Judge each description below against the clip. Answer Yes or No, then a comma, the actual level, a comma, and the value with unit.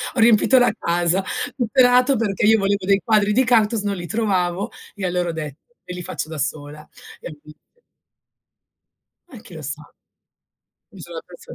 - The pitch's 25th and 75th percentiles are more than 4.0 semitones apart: Yes, average, 4.5 semitones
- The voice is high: Yes, high, 195 Hz